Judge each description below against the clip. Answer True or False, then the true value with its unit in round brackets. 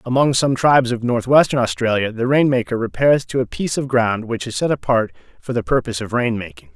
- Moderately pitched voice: False (120 Hz)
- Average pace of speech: False (220 wpm)